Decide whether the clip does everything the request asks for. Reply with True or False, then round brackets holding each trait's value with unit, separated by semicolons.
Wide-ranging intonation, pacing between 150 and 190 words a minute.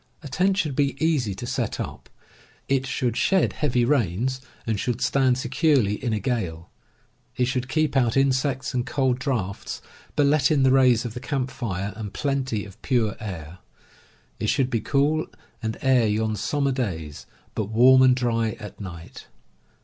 False (3.8 semitones; 170 wpm)